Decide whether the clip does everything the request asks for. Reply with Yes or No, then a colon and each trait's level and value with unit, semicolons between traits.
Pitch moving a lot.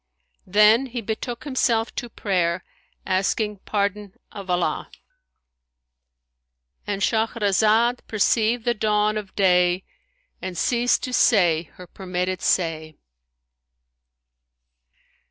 No: average, 4.1 semitones